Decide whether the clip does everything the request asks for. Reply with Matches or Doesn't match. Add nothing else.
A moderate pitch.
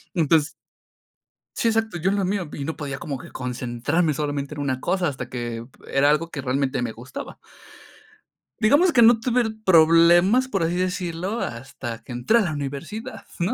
Matches